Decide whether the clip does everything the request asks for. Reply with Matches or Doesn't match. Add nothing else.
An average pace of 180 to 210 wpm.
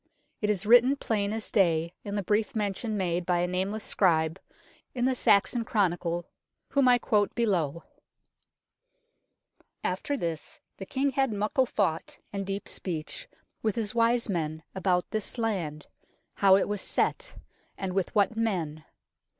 Doesn't match